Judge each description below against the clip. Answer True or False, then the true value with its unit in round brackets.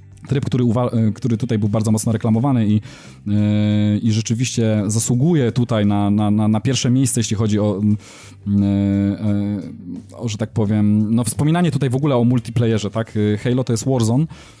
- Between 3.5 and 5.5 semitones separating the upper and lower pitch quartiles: False (2.8 semitones)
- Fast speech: True (175 wpm)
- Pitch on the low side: True (110 Hz)